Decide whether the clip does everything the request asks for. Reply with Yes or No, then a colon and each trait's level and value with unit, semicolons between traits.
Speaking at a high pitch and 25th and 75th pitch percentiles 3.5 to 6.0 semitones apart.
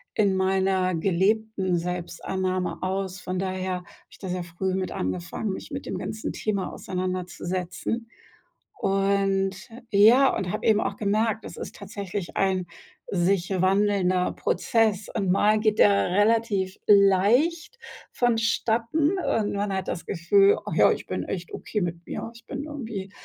No: high, 195 Hz; average, 2.8 semitones